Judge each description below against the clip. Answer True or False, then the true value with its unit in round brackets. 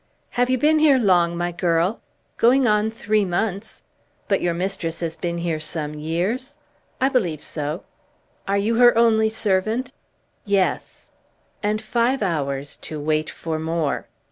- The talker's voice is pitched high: True (195 Hz)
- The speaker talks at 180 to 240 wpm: False (145 wpm)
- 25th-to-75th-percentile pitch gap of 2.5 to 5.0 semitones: False (5.6 semitones)